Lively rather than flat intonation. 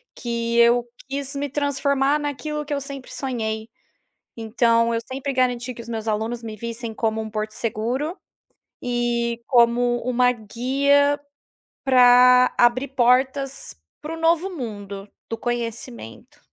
No: average, 2.9 semitones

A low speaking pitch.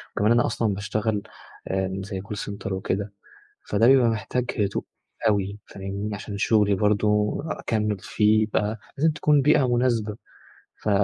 Yes: low, 105 Hz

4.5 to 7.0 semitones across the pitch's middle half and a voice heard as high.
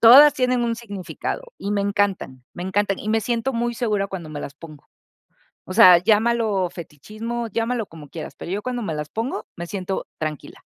Yes: average, 4.9 semitones; high, 205 Hz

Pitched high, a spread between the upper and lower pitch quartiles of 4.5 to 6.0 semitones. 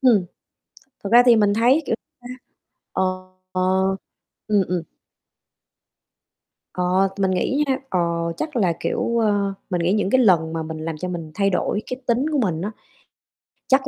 Yes: high, 200 Hz; average, 5.0 semitones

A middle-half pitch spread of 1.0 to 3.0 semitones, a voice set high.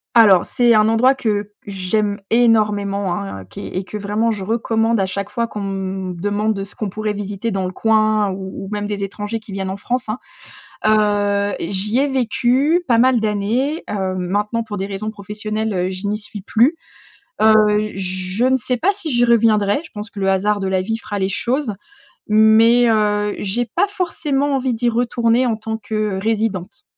Yes: narrow, 2.6 semitones; high, 215 Hz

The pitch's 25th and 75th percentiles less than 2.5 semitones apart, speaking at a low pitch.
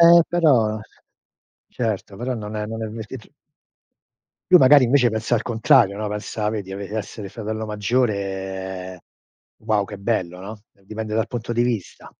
No: average, 2.9 semitones; low, 110 Hz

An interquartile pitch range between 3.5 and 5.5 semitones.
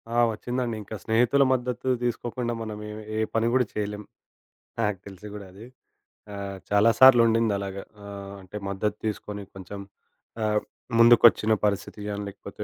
No: narrow, 2.6 semitones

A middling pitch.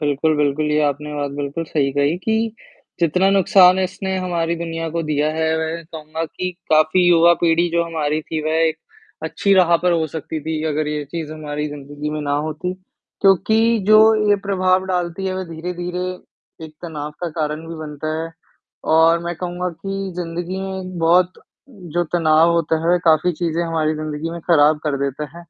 Yes: medium, 165 Hz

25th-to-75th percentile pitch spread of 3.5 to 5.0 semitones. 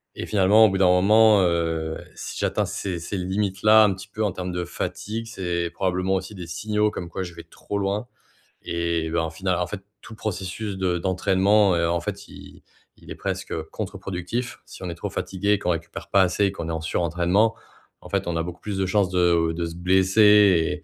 No: average, 2.9 semitones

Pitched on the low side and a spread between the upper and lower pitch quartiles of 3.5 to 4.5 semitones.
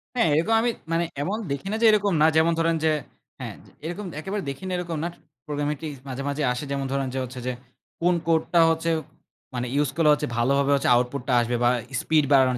No: medium, 150 Hz; average, 3.8 semitones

